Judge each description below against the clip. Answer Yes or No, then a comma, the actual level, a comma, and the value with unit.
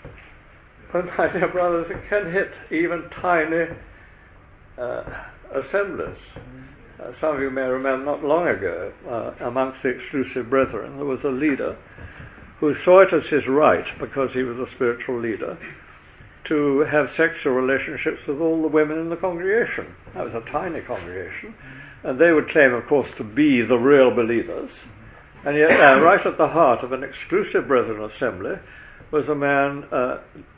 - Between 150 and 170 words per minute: Yes, average, 165 wpm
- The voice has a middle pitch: Yes, medium, 145 Hz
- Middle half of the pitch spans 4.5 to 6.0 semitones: Yes, average, 4.8 semitones